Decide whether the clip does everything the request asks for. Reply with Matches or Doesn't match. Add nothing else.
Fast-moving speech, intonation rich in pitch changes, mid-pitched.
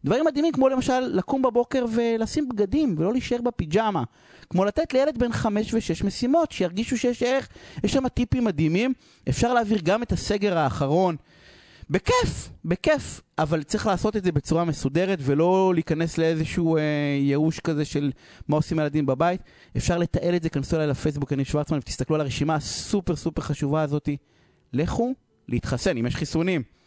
Matches